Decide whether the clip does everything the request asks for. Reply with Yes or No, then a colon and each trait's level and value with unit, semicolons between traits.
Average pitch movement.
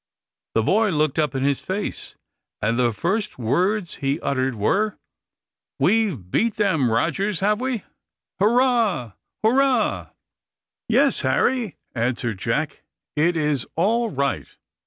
No: wide, 8.5 semitones